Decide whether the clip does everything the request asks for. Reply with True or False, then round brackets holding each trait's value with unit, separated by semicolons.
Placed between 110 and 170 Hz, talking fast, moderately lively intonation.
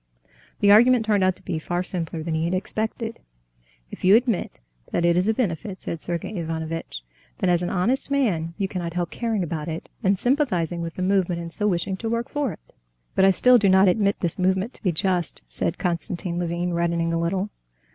False (180 Hz; 210 wpm; 3.6 semitones)